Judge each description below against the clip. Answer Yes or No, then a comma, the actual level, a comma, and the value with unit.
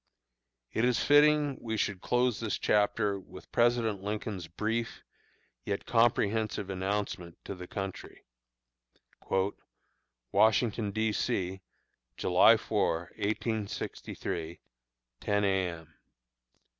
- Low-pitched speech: Yes, low, 105 Hz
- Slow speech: Yes, slow, 95 wpm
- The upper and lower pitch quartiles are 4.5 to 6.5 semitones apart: No, average, 3.1 semitones